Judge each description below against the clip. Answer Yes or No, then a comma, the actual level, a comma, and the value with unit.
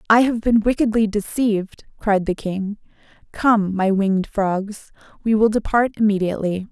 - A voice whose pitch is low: No, high, 210 Hz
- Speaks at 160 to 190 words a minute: No, average, 145 wpm